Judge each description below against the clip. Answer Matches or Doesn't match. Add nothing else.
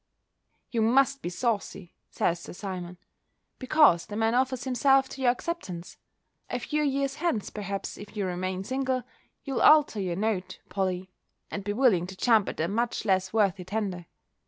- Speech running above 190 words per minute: Doesn't match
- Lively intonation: Matches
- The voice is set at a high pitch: Matches